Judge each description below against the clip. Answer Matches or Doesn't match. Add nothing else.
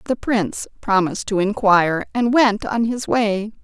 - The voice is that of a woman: Matches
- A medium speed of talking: Matches